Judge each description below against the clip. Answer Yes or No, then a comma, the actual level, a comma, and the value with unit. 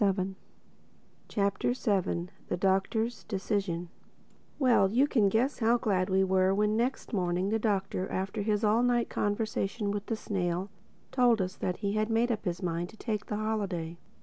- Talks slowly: No, average, 170 wpm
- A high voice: Yes, high, 205 Hz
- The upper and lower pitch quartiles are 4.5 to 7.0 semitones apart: No, average, 2.8 semitones